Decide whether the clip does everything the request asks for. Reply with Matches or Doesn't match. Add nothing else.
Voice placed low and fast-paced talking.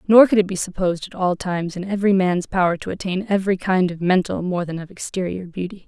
Doesn't match